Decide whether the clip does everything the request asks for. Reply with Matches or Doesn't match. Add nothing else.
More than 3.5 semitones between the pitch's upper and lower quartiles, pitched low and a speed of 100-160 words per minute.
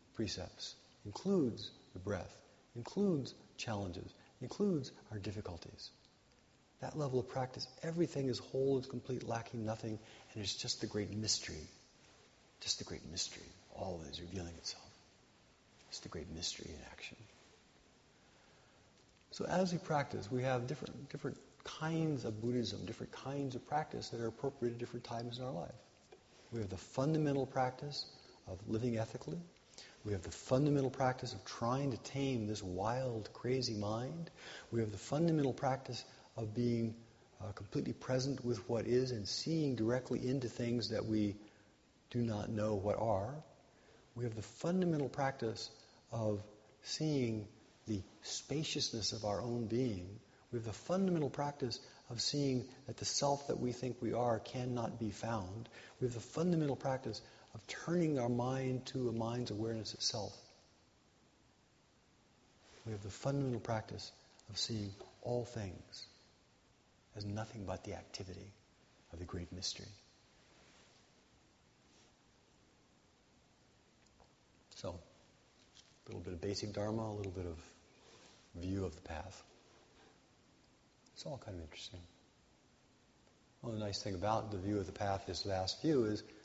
Matches